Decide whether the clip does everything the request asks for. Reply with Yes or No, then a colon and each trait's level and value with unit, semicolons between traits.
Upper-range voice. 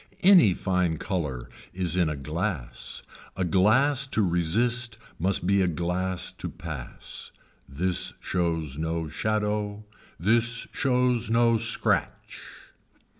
No: very low, 95 Hz